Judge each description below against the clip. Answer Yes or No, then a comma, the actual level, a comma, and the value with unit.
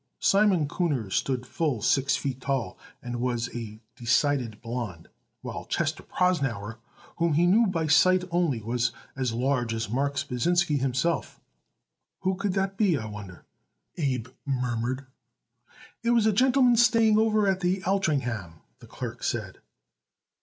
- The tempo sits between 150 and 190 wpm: No, average, 140 wpm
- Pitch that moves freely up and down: Yes, wide, 7.3 semitones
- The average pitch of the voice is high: No, medium, 140 Hz